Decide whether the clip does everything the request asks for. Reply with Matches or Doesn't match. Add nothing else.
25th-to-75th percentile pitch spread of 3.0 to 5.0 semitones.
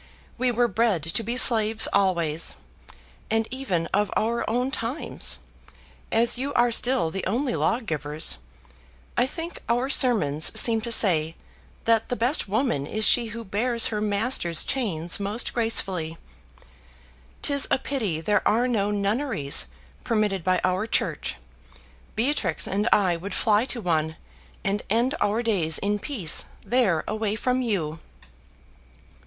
Matches